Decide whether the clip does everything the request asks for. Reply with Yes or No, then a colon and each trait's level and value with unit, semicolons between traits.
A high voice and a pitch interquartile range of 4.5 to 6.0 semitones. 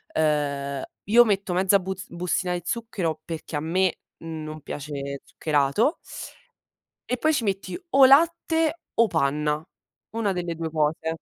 No: medium, 170 Hz; wide, 5.6 semitones